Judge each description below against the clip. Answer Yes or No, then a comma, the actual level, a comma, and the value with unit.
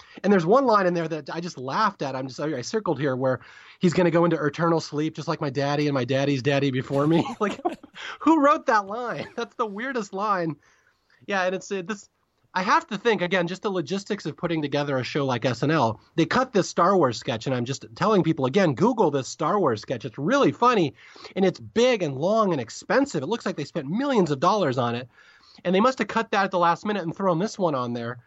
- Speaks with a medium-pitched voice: Yes, medium, 175 Hz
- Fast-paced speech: Yes, fast, 245 wpm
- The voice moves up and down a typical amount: No, wide, 6.4 semitones